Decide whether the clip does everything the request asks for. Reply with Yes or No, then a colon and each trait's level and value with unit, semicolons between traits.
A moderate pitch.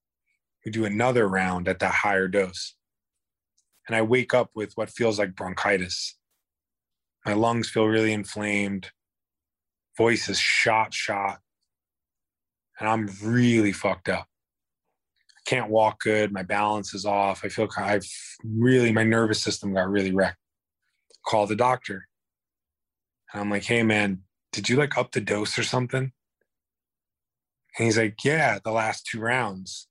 No: low, 105 Hz